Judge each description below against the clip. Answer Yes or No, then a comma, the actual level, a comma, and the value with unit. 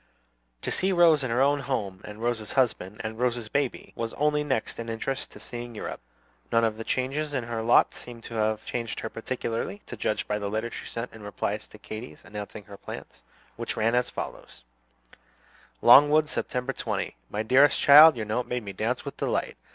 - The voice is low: Yes, low, 115 Hz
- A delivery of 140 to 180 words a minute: No, average, 200 wpm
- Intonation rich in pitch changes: No, average, 3.5 semitones